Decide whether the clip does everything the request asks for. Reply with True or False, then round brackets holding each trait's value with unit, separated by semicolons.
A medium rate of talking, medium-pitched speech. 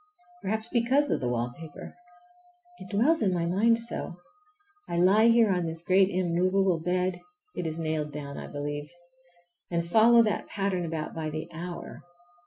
True (150 wpm; 175 Hz)